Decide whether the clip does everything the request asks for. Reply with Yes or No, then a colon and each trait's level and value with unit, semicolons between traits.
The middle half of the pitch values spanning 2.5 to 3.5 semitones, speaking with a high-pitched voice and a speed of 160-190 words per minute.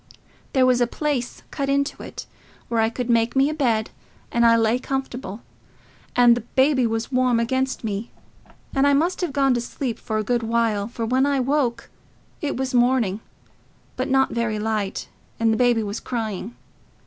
Yes: average, 2.8 semitones; high, 240 Hz; average, 185 wpm